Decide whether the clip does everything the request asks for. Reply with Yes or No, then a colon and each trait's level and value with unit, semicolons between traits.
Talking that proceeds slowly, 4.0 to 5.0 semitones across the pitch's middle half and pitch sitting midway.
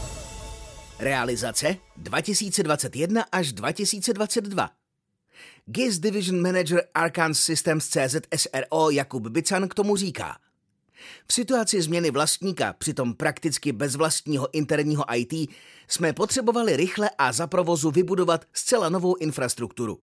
Yes: slow, 105 wpm; average, 4.7 semitones; medium, 165 Hz